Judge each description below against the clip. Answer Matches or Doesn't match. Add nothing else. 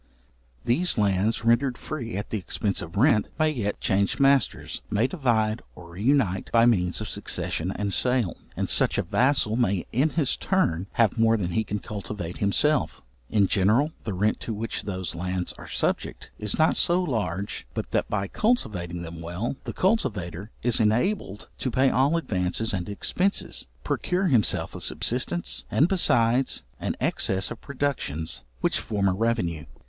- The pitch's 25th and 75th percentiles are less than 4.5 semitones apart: Doesn't match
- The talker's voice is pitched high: Doesn't match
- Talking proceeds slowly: Doesn't match